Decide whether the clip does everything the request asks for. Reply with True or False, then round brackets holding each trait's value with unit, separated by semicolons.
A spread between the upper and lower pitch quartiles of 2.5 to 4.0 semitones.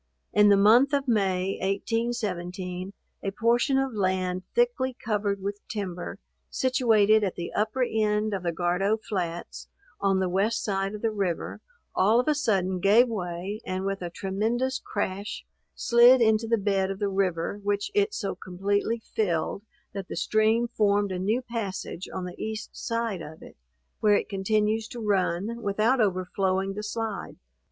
True (3.0 semitones)